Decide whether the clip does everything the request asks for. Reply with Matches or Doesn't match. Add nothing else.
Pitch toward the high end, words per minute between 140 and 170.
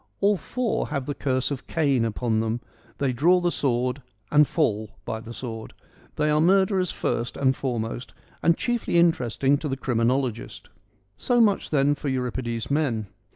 Doesn't match